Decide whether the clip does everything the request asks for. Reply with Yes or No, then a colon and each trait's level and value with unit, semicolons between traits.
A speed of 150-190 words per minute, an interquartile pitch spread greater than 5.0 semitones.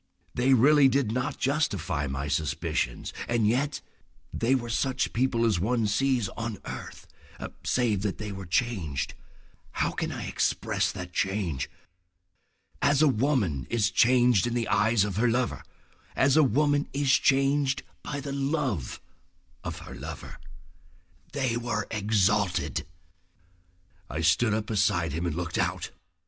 No: average, 140 wpm; wide, 5.5 semitones